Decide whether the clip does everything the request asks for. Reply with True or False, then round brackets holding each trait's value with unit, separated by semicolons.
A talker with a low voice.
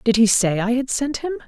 False (240 Hz)